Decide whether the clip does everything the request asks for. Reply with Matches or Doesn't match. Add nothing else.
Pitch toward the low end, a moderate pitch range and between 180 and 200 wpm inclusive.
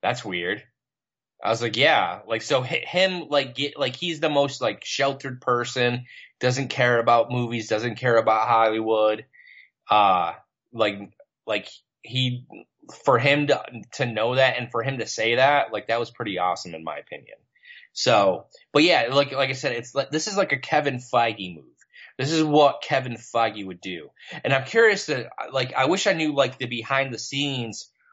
Matches